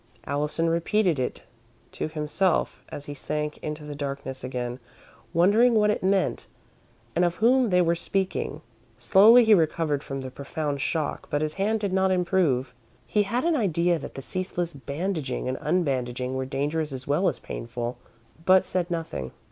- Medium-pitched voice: Yes, medium, 160 Hz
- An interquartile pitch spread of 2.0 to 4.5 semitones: No, average, 5.3 semitones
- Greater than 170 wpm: No, average, 165 wpm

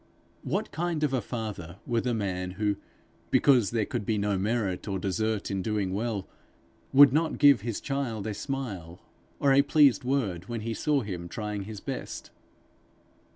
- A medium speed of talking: Yes, average, 170 wpm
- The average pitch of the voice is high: No, low, 110 Hz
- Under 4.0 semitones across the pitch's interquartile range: No, average, 5.1 semitones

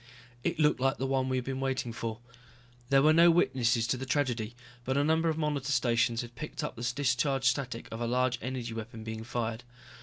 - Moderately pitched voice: No, low, 130 Hz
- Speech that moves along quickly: Yes, fast, 215 wpm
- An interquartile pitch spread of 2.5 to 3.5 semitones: Yes, average, 3.0 semitones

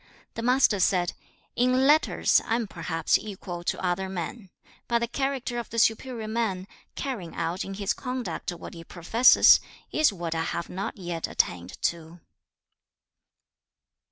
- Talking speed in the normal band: Yes, average, 150 wpm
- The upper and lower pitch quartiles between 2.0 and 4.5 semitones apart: No, wide, 5.6 semitones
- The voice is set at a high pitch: Yes, high, 195 Hz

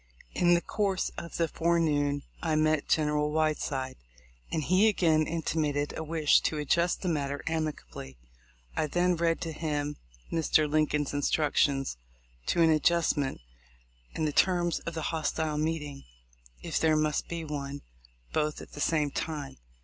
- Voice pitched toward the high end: No, medium, 155 Hz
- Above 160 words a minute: No, average, 150 wpm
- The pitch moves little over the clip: Yes, narrow, 2.1 semitones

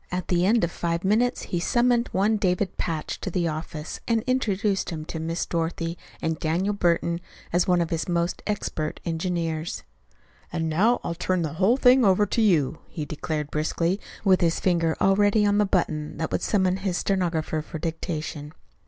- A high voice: No, medium, 175 Hz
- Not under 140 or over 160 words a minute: No, average, 180 wpm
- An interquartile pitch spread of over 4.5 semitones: No, average, 3.5 semitones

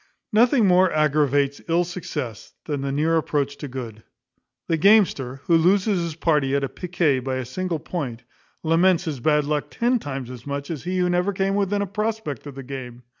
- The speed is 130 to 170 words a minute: No, average, 190 wpm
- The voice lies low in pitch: No, medium, 155 Hz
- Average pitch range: Yes, average, 4.9 semitones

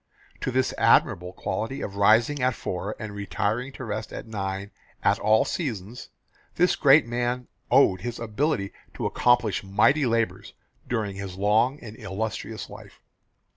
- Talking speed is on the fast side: No, average, 145 wpm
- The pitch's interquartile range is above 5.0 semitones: No, average, 3.5 semitones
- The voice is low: Yes, low, 110 Hz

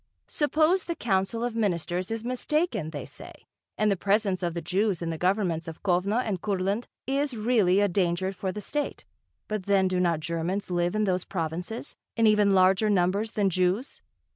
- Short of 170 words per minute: No, average, 185 wpm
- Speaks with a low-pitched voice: No, high, 195 Hz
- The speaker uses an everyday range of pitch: Yes, average, 3.5 semitones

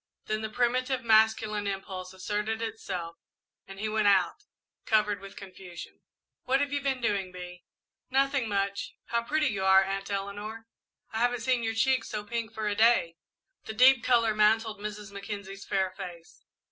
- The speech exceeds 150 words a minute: Yes, average, 170 wpm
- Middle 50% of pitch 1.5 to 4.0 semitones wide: Yes, average, 2.9 semitones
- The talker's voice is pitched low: No, high, 215 Hz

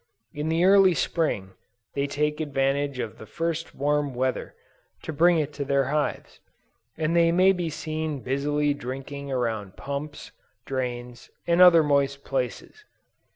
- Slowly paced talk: No, average, 145 wpm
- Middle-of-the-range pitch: Yes, medium, 145 Hz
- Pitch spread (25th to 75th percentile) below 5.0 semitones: Yes, average, 3.0 semitones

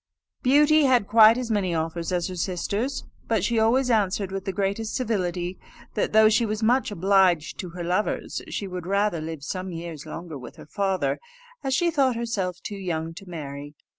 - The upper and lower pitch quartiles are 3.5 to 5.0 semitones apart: Yes, average, 4.4 semitones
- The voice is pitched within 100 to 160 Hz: No, high, 195 Hz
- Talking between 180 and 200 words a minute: Yes, average, 190 wpm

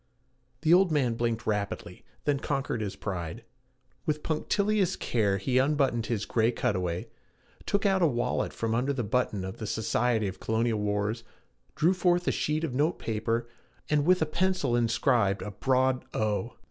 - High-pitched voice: No, low, 120 Hz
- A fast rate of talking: No, average, 165 wpm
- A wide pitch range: Yes, wide, 5.8 semitones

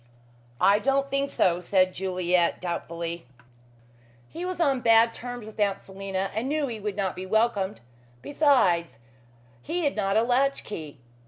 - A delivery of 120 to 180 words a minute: Yes, average, 155 wpm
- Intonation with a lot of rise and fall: Yes, wide, 6.0 semitones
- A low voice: No, high, 210 Hz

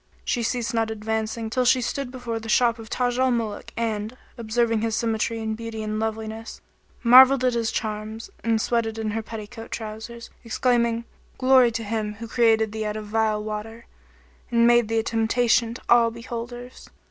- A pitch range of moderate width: No, narrow, 1.4 semitones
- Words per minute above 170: Yes, average, 180 wpm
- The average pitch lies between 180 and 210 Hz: No, high, 225 Hz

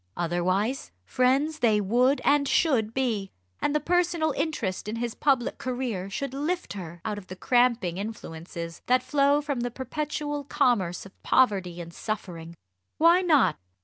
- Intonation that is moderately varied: No, wide, 6.8 semitones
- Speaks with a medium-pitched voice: No, high, 245 Hz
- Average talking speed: Yes, average, 150 wpm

